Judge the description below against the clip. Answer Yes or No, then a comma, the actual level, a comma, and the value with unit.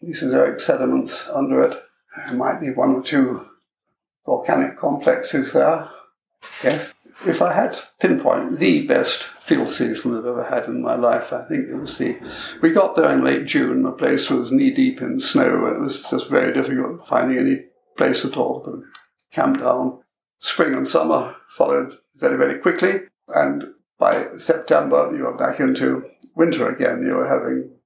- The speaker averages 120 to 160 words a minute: No, average, 170 wpm